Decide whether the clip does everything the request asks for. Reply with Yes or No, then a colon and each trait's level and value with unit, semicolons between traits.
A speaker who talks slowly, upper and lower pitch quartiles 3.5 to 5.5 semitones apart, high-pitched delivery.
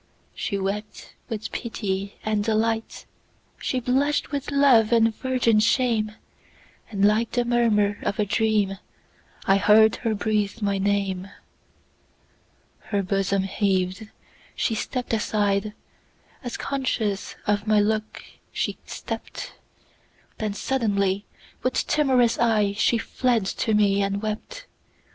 No: slow, 100 wpm; narrow, 2.6 semitones; high, 215 Hz